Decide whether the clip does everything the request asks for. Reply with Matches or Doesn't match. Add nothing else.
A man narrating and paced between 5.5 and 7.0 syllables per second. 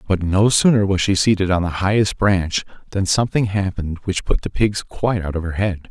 Matches